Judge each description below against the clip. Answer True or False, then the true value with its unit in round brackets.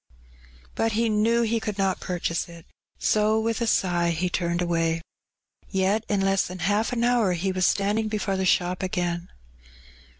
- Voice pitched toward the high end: True (195 Hz)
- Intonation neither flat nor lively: True (3.6 semitones)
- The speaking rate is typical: True (170 wpm)